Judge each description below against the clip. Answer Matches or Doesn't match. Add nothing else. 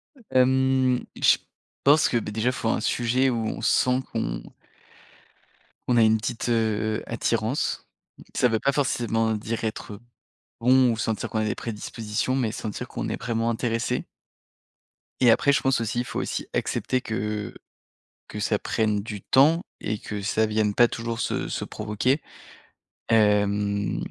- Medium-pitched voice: Doesn't match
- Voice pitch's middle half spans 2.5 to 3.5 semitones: Matches